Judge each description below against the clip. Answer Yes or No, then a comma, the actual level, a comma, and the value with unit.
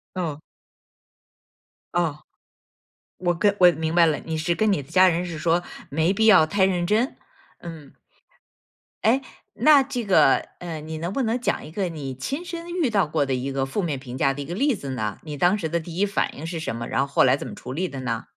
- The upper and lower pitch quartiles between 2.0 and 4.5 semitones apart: No, wide, 5.6 semitones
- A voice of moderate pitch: Yes, medium, 170 Hz